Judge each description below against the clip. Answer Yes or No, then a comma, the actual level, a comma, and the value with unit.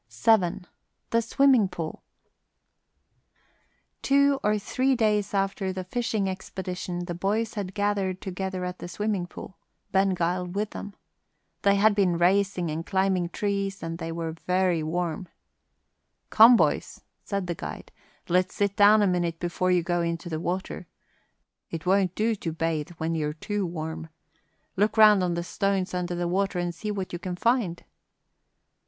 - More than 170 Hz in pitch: Yes, medium, 185 Hz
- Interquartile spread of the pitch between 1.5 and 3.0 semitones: Yes, average, 2.7 semitones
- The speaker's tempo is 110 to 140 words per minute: No, average, 155 wpm